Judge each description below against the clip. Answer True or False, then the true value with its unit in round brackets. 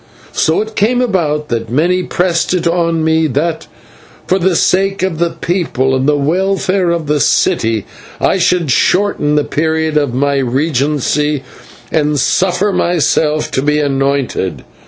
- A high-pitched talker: False (160 Hz)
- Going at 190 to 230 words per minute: False (150 wpm)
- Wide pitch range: False (3.9 semitones)